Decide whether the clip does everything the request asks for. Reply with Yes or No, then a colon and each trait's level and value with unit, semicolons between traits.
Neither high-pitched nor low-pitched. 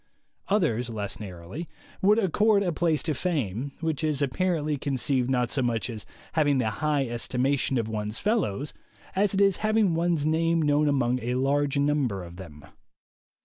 Yes: medium, 145 Hz